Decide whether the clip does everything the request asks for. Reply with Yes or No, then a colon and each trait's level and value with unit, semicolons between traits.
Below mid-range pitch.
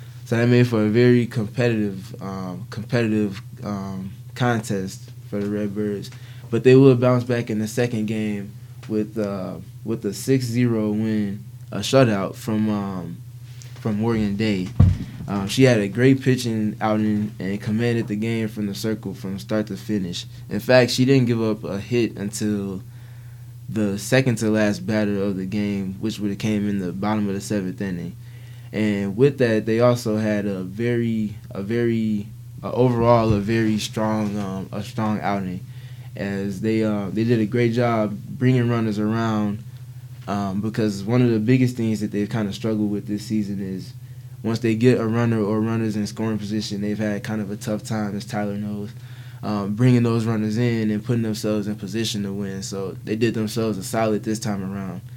Yes: low, 110 Hz